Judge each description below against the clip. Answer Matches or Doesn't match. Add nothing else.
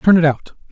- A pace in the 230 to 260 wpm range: Matches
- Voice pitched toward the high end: Doesn't match